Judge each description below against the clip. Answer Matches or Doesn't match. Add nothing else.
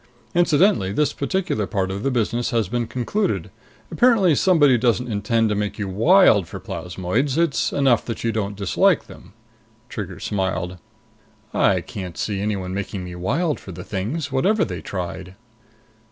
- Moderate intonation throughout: Doesn't match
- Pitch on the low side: Matches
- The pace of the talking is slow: Doesn't match